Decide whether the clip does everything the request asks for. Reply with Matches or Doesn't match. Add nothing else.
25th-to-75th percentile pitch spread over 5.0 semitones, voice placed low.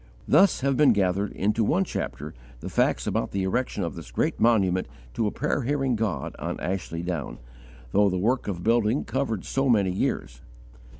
Matches